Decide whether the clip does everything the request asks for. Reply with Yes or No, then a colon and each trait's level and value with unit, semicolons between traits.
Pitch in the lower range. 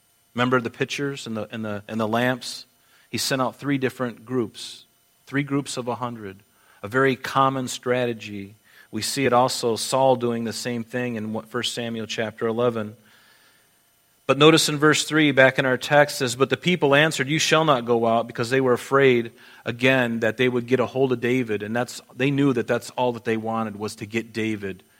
Yes: low, 125 Hz